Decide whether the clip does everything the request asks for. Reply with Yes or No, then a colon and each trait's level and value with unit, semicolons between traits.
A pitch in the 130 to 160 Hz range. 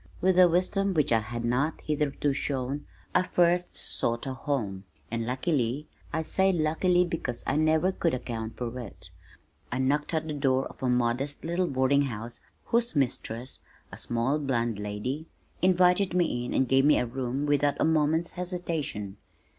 Yes: medium, 140 Hz